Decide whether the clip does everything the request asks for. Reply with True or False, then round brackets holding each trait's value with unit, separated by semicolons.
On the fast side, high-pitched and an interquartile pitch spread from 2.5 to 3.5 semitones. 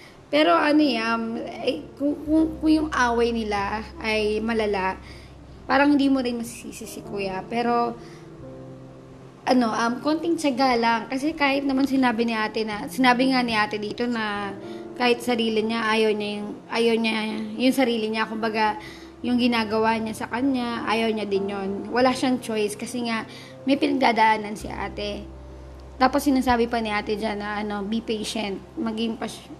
True (160 wpm; 230 Hz; 3.2 semitones)